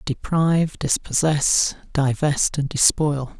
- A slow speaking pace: Yes, slow, 90 wpm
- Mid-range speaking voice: Yes, medium, 145 Hz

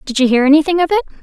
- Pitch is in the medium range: No, very high, 290 Hz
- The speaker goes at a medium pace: No, fast, 295 wpm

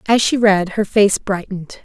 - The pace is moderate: Yes, average, 195 wpm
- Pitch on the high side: Yes, high, 200 Hz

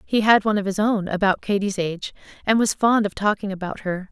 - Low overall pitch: No, high, 200 Hz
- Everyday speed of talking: No, fast, 235 wpm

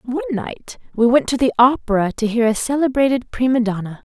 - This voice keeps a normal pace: Yes, average, 190 wpm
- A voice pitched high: Yes, high, 240 Hz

